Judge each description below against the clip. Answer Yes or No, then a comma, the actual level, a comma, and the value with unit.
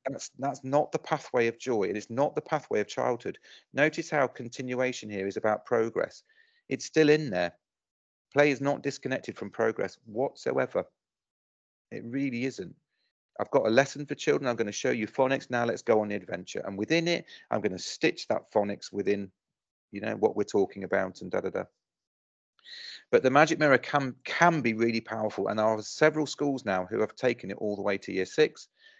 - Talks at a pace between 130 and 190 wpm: No, fast, 205 wpm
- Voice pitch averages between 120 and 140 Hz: Yes, low, 130 Hz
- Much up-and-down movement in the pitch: Yes, wide, 5.8 semitones